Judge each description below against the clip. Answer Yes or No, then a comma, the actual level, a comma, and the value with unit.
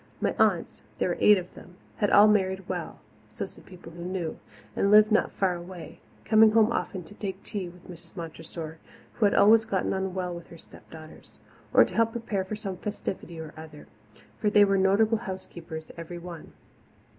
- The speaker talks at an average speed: Yes, average, 195 wpm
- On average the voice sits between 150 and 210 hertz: Yes, high, 190 Hz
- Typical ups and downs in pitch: Yes, average, 3.3 semitones